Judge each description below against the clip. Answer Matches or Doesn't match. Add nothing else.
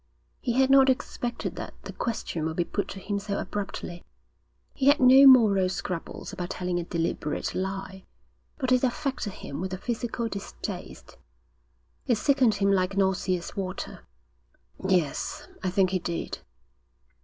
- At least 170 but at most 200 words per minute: Doesn't match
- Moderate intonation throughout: Matches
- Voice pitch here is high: Matches